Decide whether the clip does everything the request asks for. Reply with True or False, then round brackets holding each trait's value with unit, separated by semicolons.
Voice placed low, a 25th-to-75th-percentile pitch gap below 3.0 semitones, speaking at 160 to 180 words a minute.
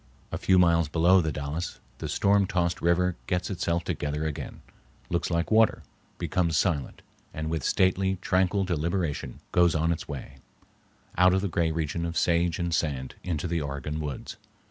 True (85 Hz; 2.5 semitones; 165 wpm)